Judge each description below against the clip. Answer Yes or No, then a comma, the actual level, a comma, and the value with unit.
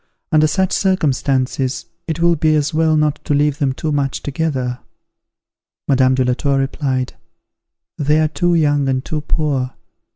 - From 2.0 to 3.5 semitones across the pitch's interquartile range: Yes, average, 2.8 semitones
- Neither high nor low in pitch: Yes, medium, 145 Hz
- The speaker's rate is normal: Yes, average, 160 wpm